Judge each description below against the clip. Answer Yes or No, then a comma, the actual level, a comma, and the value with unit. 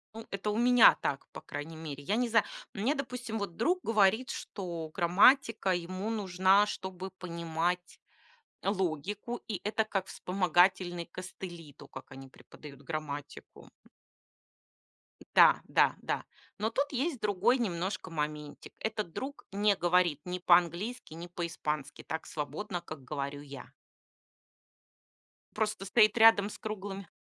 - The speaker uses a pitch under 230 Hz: Yes, medium, 185 Hz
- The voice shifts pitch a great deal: No, average, 4.5 semitones